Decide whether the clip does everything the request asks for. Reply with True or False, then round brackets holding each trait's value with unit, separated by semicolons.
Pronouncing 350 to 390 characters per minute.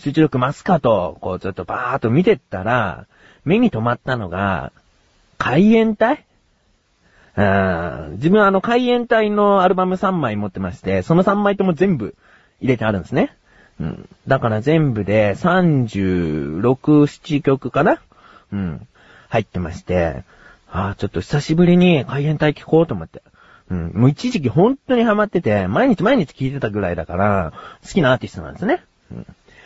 False (310 characters per minute)